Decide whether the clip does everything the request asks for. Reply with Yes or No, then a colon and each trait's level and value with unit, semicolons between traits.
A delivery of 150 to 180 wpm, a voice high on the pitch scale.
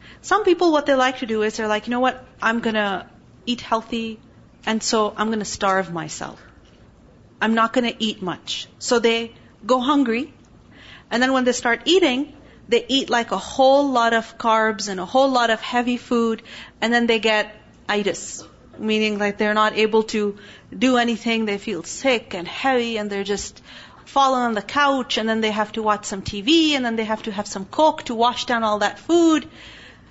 No: average, 200 wpm; high, 225 Hz